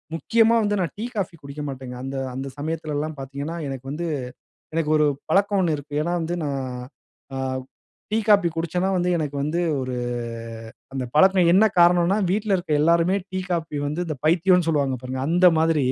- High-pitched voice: No, medium, 165 Hz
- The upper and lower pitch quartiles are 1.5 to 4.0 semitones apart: Yes, average, 3.7 semitones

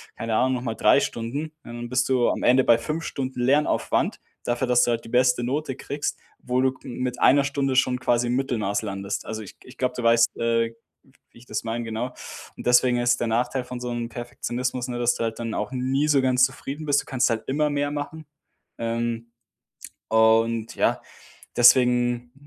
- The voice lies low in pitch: Yes, low, 125 Hz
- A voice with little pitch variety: Yes, narrow, 2.0 semitones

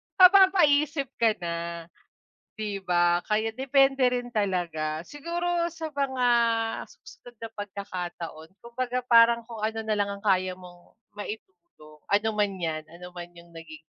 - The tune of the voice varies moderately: No, wide, 7.3 semitones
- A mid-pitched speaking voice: No, high, 215 Hz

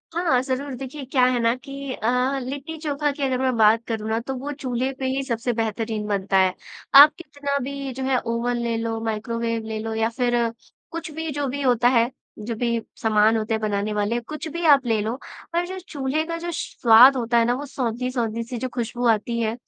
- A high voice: Yes, high, 245 Hz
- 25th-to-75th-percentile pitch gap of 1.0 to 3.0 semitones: No, average, 3.4 semitones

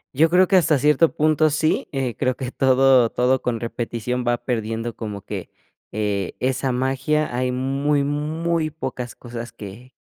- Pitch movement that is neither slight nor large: Yes, average, 3.7 semitones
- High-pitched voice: No, low, 130 Hz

